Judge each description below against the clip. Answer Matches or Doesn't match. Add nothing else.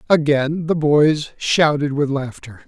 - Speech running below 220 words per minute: Matches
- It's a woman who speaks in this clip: Doesn't match